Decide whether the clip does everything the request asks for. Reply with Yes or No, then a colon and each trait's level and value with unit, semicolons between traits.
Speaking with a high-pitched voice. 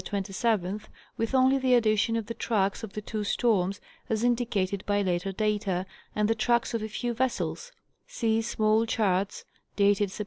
Yes: high, 215 Hz